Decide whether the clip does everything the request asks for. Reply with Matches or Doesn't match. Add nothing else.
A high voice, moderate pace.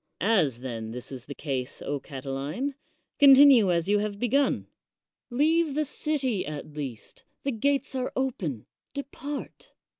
Doesn't match